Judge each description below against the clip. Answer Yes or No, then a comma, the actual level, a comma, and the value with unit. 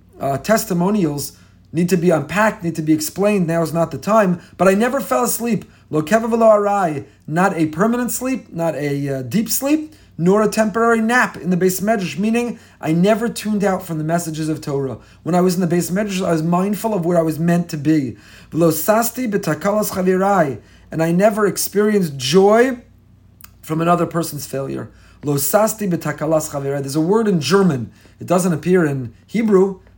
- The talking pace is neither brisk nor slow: Yes, average, 175 wpm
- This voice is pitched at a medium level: Yes, medium, 175 Hz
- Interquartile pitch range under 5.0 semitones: No, wide, 5.4 semitones